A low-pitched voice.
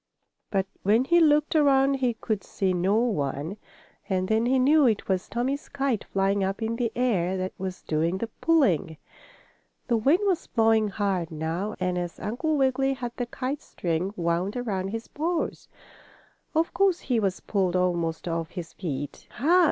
No: high, 215 Hz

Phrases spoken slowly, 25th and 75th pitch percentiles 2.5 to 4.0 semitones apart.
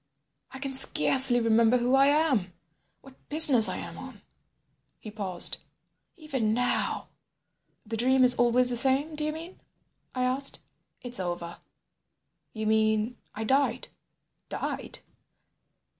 Yes: slow, 130 wpm; average, 3.6 semitones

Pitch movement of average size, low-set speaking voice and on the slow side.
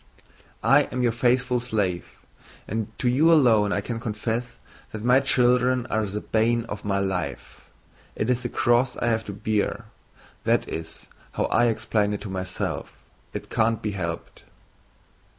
No: average, 3.1 semitones; low, 110 Hz; average, 160 wpm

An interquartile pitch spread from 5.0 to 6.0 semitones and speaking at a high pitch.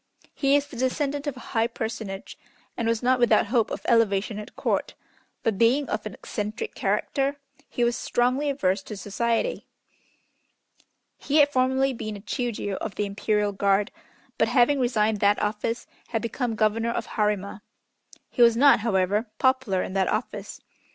No: average, 3.7 semitones; high, 230 Hz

